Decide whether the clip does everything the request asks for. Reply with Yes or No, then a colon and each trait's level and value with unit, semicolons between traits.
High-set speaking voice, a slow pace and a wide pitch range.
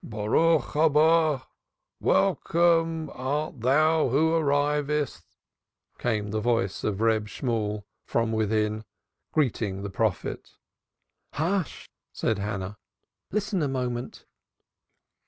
No: low, 130 Hz; slow, 95 wpm; wide, 6.3 semitones